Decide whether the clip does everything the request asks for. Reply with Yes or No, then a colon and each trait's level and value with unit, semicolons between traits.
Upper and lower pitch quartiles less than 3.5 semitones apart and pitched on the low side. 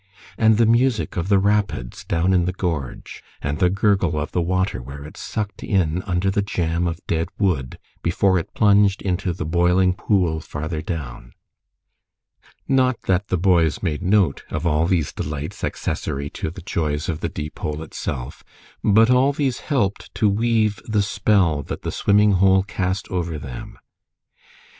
No: average, 4.2 semitones; very low, 90 Hz